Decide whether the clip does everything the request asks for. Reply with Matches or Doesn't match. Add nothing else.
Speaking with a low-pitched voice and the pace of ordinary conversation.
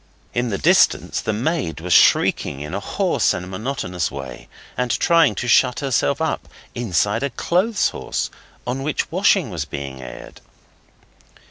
Matches